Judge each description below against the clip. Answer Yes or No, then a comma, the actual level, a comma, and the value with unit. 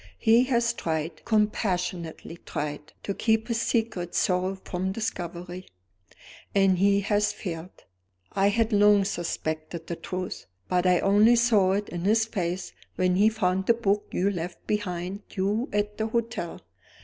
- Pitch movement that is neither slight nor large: Yes, average, 3.4 semitones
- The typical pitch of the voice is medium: No, high, 195 Hz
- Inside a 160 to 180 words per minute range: No, average, 150 wpm